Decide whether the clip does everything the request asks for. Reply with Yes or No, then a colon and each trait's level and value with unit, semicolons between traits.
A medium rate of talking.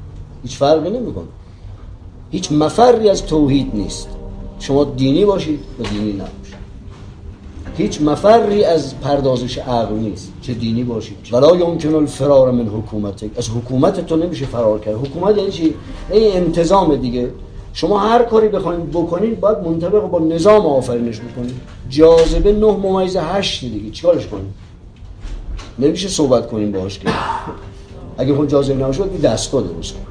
Yes: average, 140 wpm